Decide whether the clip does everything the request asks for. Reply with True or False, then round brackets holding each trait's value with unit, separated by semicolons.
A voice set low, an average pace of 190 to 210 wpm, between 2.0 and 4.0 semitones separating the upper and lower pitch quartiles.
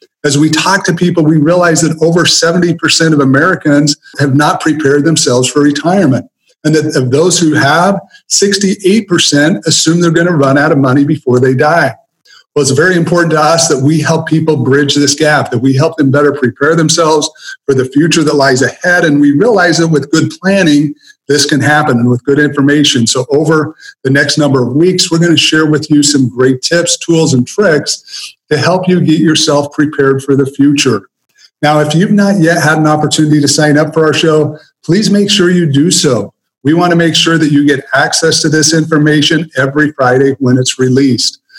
False (155 Hz; 205 wpm; 2.8 semitones)